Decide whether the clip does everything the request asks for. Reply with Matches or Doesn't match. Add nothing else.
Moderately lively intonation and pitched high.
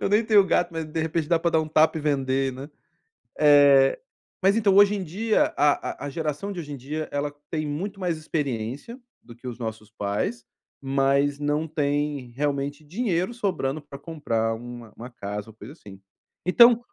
Doesn't match